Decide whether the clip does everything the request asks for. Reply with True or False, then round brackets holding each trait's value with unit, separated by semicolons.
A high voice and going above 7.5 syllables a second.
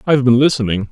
False (120 Hz; 7.8 syllables/s)